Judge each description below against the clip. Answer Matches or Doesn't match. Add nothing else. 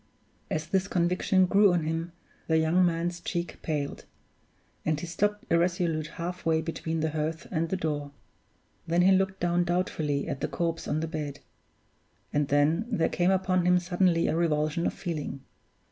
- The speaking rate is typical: Matches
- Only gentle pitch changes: Matches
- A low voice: Doesn't match